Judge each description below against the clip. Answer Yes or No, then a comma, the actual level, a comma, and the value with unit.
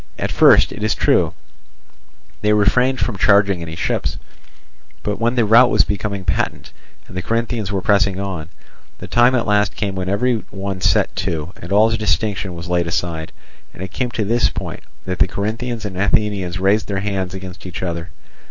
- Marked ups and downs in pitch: No, average, 2.8 semitones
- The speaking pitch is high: No, low, 100 Hz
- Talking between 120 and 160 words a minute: No, average, 185 wpm